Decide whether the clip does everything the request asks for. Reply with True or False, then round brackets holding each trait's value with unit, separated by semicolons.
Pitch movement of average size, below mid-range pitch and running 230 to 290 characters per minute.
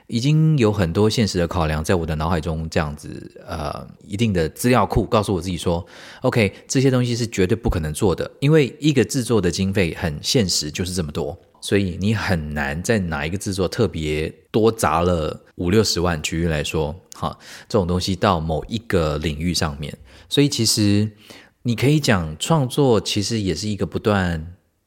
True (5.0 semitones; 100 Hz; 285 characters per minute)